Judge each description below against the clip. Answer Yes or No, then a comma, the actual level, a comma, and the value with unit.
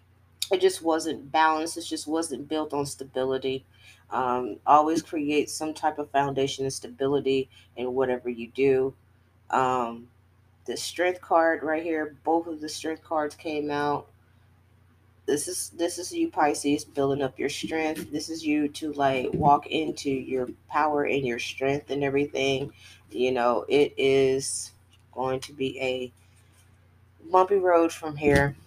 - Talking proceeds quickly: No, average, 150 wpm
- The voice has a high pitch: No, medium, 140 Hz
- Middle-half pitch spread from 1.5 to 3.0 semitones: No, average, 4.2 semitones